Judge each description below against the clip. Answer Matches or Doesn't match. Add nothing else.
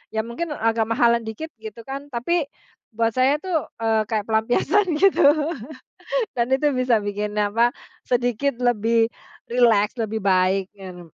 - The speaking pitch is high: Matches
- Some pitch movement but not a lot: Matches